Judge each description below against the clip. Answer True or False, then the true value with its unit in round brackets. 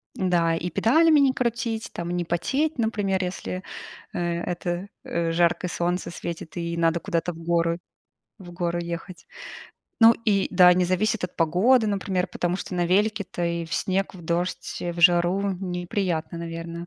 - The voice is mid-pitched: True (175 Hz)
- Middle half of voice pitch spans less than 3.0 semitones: True (2.4 semitones)